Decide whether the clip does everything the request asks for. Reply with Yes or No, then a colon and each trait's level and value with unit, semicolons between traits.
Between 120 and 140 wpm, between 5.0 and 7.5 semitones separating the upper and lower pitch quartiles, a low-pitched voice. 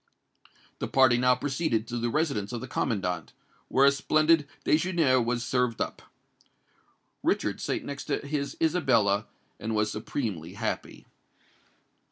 No: slow, 135 wpm; average, 4.5 semitones; low, 125 Hz